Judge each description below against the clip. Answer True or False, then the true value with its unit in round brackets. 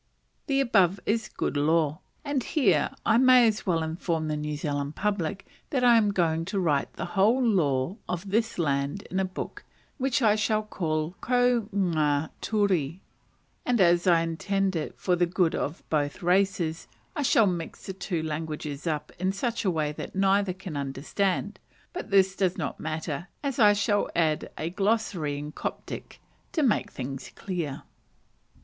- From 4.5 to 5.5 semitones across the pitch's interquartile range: True (4.8 semitones)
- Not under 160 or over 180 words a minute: True (170 wpm)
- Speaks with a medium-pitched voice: True (180 Hz)